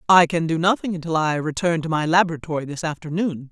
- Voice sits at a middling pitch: Yes, medium, 165 Hz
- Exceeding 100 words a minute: Yes, fast, 205 wpm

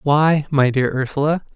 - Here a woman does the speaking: No, male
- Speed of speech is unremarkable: Yes, average, 155 wpm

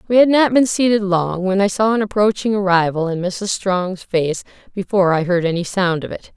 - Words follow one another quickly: Yes, fast, 215 wpm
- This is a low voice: No, high, 195 Hz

